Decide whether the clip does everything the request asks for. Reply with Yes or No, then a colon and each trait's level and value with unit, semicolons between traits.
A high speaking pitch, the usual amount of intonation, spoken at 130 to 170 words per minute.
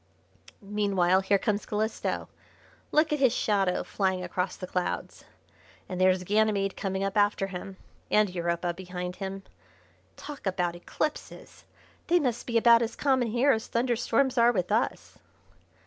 Yes: high, 200 Hz; average, 4.0 semitones; average, 145 wpm